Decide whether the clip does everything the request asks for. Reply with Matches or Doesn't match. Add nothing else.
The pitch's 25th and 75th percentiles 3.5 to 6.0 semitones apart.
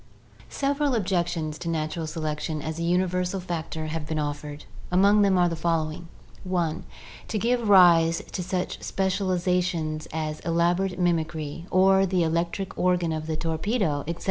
Doesn't match